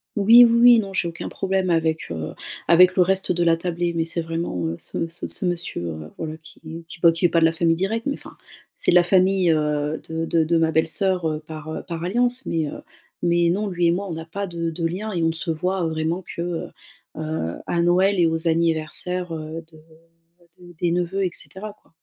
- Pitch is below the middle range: No, medium, 170 Hz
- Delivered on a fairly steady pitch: Yes, narrow, 2.2 semitones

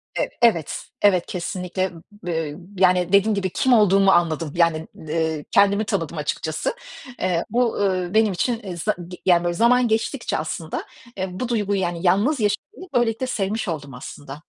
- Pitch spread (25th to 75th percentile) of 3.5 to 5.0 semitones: Yes, average, 4.4 semitones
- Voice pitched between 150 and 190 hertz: Yes, medium, 185 Hz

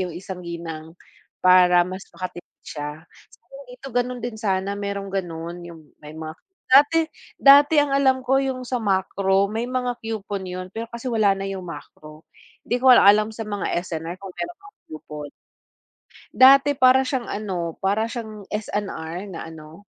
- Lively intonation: Yes, wide, 6.1 semitones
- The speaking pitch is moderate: No, high, 200 Hz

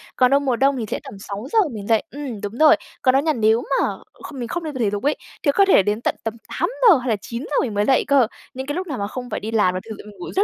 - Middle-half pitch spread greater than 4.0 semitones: Yes, average, 4.8 semitones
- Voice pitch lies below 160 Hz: No, very high, 250 Hz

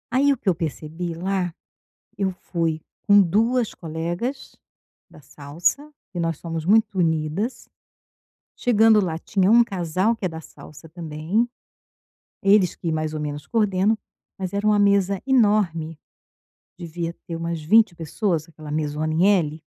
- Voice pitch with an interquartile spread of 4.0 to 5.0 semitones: Yes, average, 4.3 semitones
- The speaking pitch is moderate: Yes, medium, 175 Hz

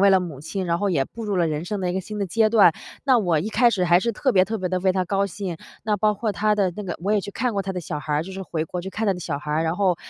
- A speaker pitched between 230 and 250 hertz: No, high, 190 Hz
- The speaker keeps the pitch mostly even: No, average, 3.2 semitones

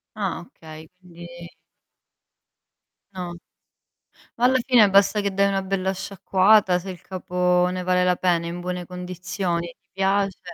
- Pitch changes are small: Yes, narrow, 1.7 semitones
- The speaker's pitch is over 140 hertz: Yes, medium, 185 Hz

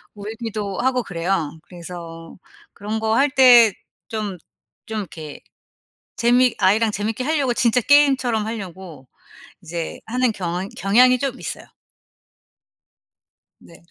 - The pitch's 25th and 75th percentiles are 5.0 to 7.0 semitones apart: Yes, wide, 5.5 semitones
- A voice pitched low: No, high, 215 Hz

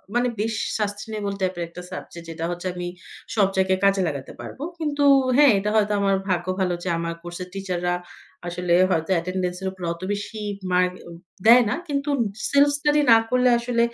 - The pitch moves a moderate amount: Yes, average, 4.4 semitones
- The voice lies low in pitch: No, high, 190 Hz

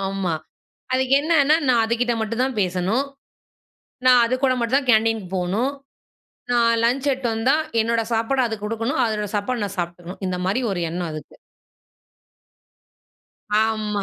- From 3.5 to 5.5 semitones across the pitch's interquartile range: Yes, average, 4.2 semitones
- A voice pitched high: Yes, high, 225 Hz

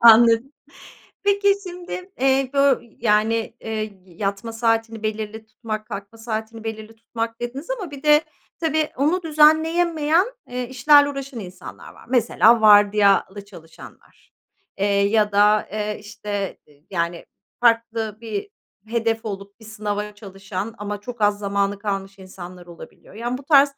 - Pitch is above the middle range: Yes, high, 220 Hz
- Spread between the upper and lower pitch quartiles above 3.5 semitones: Yes, average, 4.1 semitones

